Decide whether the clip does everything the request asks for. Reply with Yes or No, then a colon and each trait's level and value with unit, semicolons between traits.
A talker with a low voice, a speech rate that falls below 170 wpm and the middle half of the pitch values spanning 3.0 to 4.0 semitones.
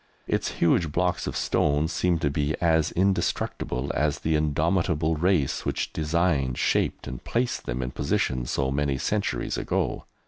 Yes: very low, 75 Hz; average, 150 wpm; average, 3.5 semitones